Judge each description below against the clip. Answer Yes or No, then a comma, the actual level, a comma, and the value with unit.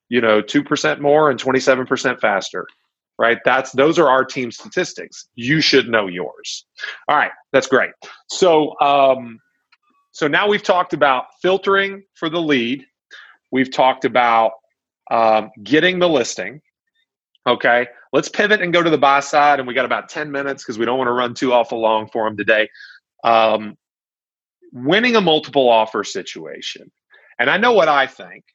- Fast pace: No, average, 170 wpm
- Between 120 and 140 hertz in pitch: Yes, low, 135 Hz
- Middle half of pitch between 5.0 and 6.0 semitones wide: Yes, wide, 5.6 semitones